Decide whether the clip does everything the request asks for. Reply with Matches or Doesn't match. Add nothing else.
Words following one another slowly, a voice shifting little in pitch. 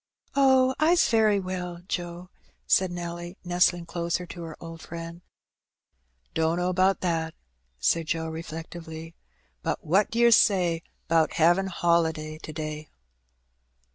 Matches